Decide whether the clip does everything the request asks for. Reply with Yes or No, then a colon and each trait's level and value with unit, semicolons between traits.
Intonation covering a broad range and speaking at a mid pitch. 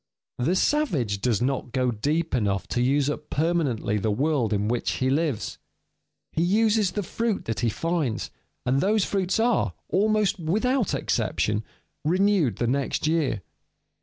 Yes: wide, 7.8 semitones; medium, 150 Hz